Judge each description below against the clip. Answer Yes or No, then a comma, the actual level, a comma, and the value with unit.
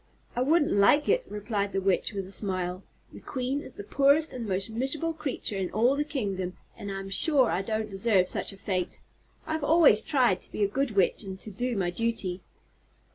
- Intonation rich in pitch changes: Yes, wide, 5.7 semitones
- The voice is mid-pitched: No, high, 215 Hz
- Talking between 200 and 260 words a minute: Yes, fast, 205 wpm